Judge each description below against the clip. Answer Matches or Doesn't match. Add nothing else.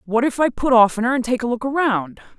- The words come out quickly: Matches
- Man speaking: Doesn't match